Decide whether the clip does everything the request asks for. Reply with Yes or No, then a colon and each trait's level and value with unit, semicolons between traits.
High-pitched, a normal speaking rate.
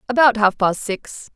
Yes: high, 220 Hz; average, 175 wpm